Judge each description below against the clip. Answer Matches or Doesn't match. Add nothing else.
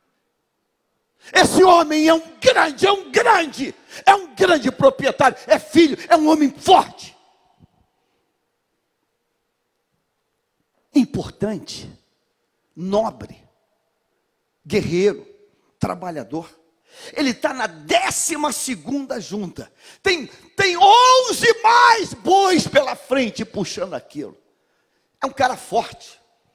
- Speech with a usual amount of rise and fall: Doesn't match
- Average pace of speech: Doesn't match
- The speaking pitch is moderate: Doesn't match